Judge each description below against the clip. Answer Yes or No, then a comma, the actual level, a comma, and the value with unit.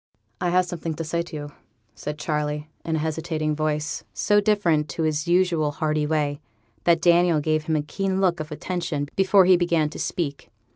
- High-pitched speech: No, medium, 160 Hz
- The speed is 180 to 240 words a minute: Yes, average, 190 wpm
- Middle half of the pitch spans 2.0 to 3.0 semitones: Yes, narrow, 2.5 semitones